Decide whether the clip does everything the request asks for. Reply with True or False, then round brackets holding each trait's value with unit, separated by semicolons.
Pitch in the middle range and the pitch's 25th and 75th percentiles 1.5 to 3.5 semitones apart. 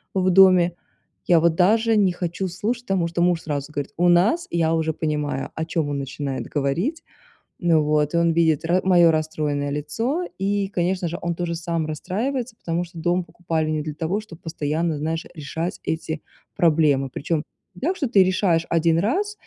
True (170 Hz; 3.0 semitones)